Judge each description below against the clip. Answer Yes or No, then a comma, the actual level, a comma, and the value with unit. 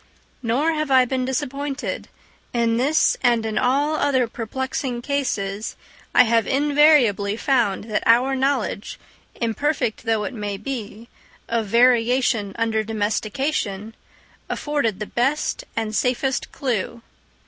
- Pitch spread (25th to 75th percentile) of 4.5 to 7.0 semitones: No, average, 3.6 semitones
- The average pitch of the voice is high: Yes, high, 240 Hz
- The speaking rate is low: Yes, slow, 115 wpm